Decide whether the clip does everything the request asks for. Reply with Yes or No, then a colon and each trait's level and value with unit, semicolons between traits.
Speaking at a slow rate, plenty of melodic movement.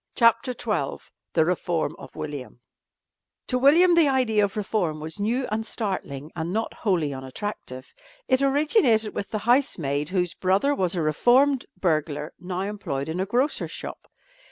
No: average, 155 wpm; wide, 7.4 semitones